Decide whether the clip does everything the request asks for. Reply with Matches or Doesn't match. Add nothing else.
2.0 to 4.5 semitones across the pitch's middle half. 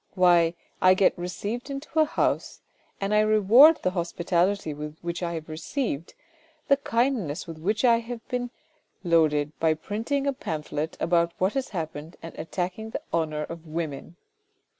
Doesn't match